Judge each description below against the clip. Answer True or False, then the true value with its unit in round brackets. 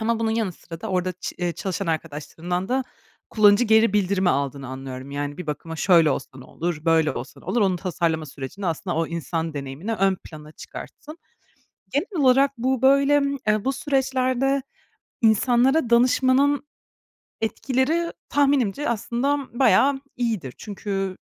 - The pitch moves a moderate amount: False (7.9 semitones)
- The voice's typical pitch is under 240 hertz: True (205 Hz)